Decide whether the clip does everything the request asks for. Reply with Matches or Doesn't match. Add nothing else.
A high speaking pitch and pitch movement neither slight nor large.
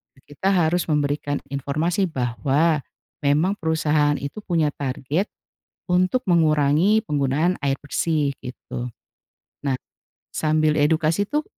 Doesn't match